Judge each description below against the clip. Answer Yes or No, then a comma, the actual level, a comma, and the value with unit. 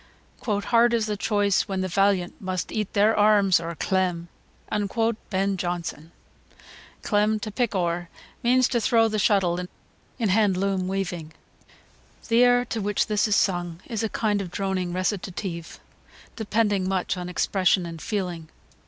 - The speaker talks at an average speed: Yes, average, 155 wpm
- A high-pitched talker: Yes, high, 195 Hz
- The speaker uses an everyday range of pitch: Yes, average, 3.0 semitones